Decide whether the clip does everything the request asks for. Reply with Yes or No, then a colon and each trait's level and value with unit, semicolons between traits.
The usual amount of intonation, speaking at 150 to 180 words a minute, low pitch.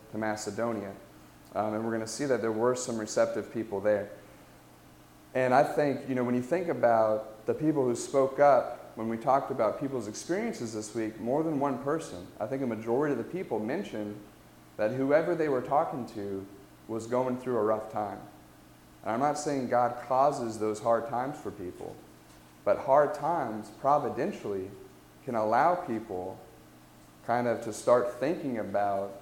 Yes: average, 3.8 semitones; average, 175 wpm; low, 115 Hz